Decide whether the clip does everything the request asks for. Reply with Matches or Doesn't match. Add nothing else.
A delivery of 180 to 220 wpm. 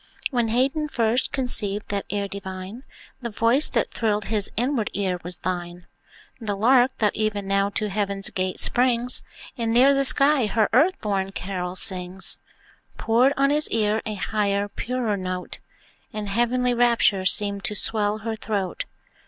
Doesn't match